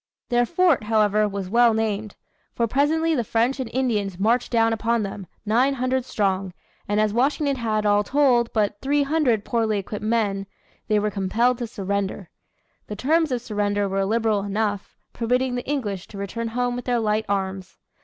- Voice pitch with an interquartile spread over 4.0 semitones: No, average, 3.3 semitones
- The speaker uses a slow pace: No, average, 175 wpm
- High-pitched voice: Yes, high, 225 Hz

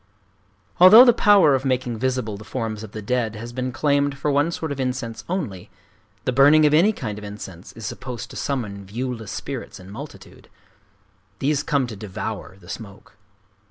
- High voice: No, low, 125 Hz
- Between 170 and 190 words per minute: Yes, average, 180 wpm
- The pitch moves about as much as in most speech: Yes, average, 4.9 semitones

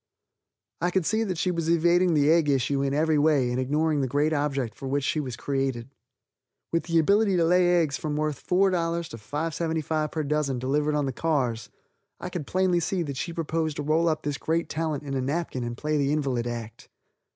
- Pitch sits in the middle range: Yes, medium, 150 Hz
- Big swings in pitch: No, average, 3.3 semitones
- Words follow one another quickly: Yes, fast, 210 wpm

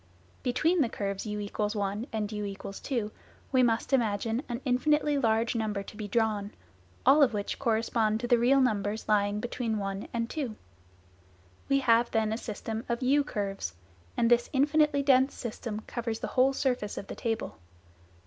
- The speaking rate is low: No, average, 170 wpm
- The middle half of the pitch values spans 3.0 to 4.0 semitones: Yes, average, 3.4 semitones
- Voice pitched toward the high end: Yes, high, 230 Hz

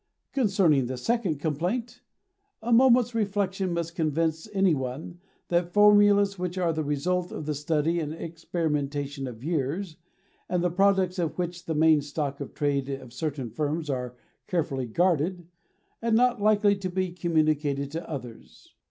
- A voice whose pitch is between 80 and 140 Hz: No, medium, 165 Hz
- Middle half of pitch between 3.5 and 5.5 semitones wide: Yes, average, 4.7 semitones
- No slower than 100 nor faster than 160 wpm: Yes, average, 155 wpm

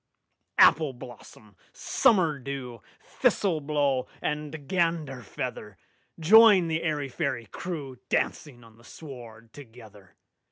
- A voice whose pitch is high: No, medium, 140 Hz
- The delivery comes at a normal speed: No, slow, 70 wpm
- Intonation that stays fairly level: No, average, 4.8 semitones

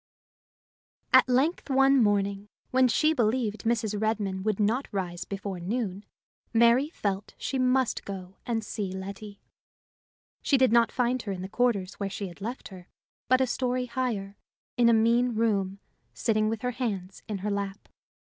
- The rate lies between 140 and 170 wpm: Yes, average, 165 wpm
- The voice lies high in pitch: Yes, high, 220 Hz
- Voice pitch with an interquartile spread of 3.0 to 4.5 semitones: Yes, average, 4.0 semitones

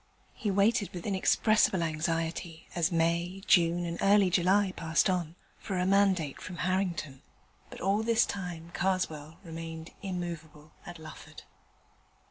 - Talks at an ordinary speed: No, slow, 130 wpm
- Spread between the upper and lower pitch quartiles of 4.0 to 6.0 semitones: No, average, 2.8 semitones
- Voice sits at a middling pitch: Yes, medium, 175 Hz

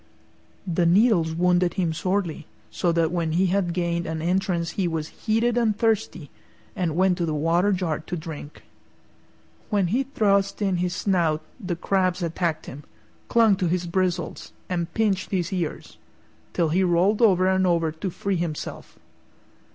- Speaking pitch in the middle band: Yes, medium, 180 Hz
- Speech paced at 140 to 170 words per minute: Yes, average, 160 wpm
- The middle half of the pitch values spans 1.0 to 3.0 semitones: Yes, narrow, 2.5 semitones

